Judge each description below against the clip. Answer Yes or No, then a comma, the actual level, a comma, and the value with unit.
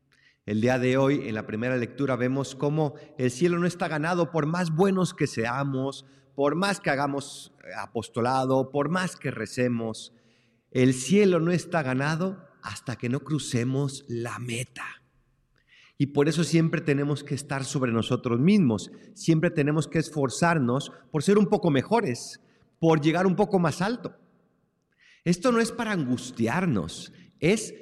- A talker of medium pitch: Yes, medium, 145 Hz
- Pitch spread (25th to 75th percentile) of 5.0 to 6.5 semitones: Yes, wide, 5.4 semitones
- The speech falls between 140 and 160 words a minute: Yes, average, 155 wpm